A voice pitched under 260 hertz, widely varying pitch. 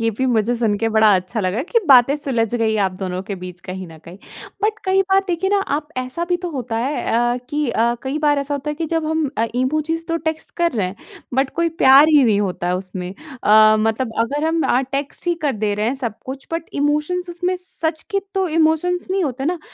No: very high, 270 Hz; wide, 6.4 semitones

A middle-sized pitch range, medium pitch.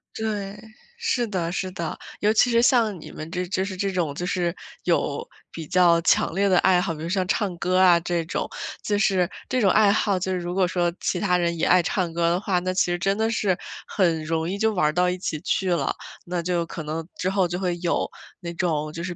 No: narrow, 2.3 semitones; medium, 180 Hz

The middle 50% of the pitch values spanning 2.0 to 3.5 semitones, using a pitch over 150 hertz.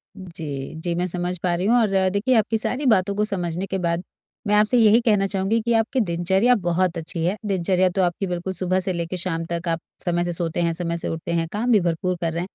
Yes: average, 3.2 semitones; medium, 185 Hz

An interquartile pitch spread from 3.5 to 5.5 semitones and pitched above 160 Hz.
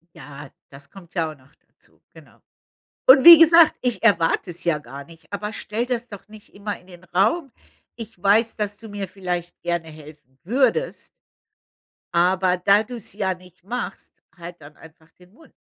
Yes: average, 4.8 semitones; high, 190 Hz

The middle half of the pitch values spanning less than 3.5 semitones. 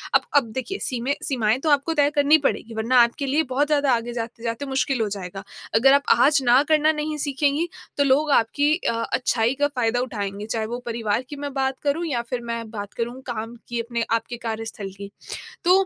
No: average, 3.9 semitones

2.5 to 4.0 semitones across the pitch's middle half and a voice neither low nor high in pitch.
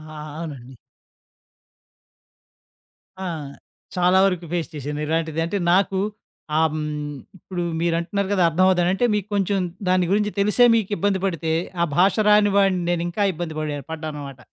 Yes: average, 3.7 semitones; medium, 175 Hz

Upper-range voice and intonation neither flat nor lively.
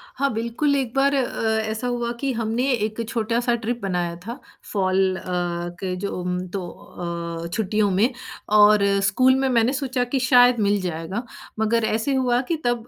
Yes: high, 230 Hz; average, 3.5 semitones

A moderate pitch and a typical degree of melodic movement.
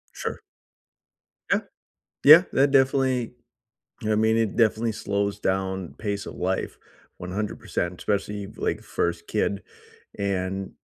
No: low, 100 Hz; average, 3.0 semitones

